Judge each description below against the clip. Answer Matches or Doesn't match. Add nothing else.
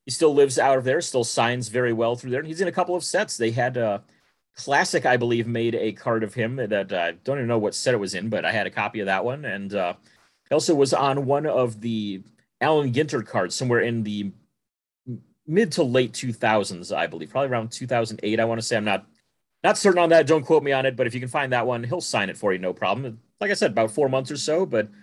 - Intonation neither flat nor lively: Matches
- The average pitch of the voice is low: Matches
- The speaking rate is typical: Doesn't match